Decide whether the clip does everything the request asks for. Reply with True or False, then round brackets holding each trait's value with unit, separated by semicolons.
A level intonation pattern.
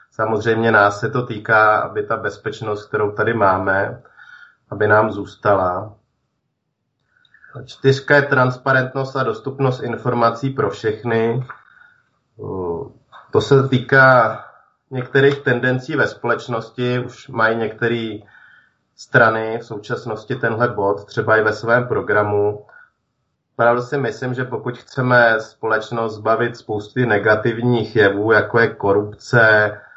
False (3.1 semitones)